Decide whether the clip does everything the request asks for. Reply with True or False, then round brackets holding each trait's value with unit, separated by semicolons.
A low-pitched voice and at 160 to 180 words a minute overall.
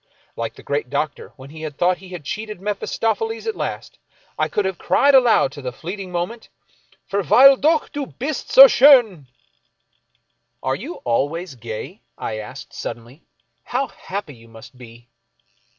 False (180 Hz; 165 wpm)